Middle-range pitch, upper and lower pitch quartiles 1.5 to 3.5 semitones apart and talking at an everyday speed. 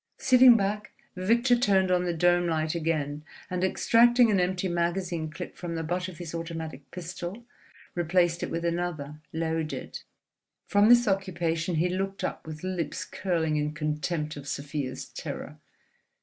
Yes: medium, 175 Hz; average, 2.9 semitones; average, 150 wpm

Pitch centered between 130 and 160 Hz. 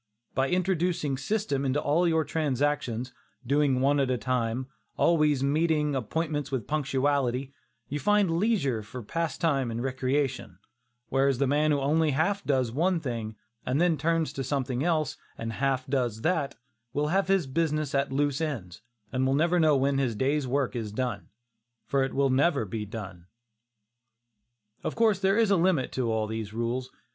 Yes: medium, 140 Hz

